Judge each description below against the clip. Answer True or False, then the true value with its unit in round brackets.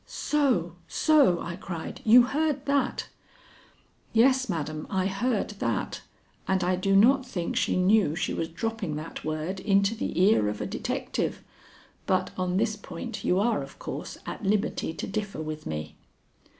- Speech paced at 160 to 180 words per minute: True (165 wpm)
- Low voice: False (190 Hz)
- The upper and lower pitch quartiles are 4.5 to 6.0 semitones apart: True (5.1 semitones)